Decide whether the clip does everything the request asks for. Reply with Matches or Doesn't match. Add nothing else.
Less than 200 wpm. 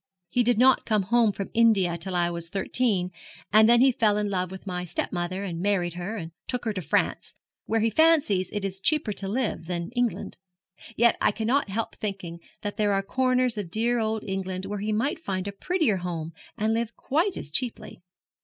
Doesn't match